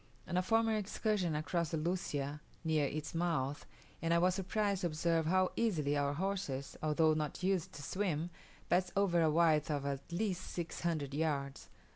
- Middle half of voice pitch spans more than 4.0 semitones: No, average, 3.6 semitones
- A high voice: No, medium, 165 Hz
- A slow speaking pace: No, average, 180 wpm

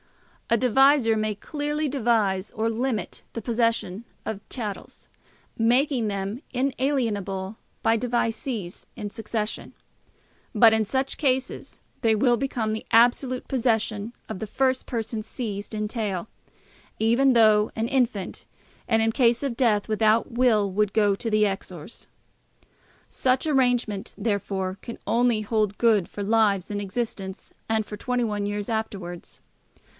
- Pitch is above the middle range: Yes, high, 225 Hz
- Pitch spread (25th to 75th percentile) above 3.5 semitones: No, average, 3.0 semitones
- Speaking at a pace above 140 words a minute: No, slow, 135 wpm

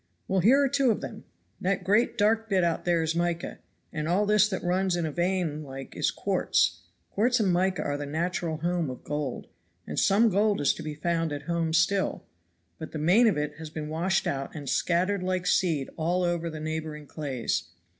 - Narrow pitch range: No, average, 3.7 semitones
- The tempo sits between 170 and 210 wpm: Yes, fast, 205 wpm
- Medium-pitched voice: Yes, medium, 170 Hz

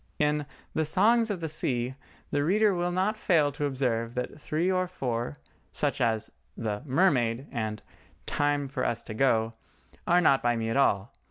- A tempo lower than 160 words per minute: No, average, 175 wpm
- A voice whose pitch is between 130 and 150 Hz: Yes, medium, 140 Hz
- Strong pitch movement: Yes, wide, 6.7 semitones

